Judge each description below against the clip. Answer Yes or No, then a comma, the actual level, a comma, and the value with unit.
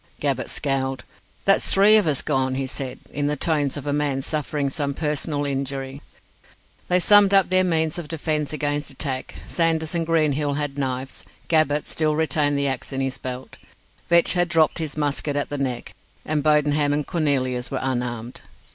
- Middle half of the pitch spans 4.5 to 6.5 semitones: No, average, 2.7 semitones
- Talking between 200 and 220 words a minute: No, average, 175 wpm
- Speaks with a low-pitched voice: No, medium, 145 Hz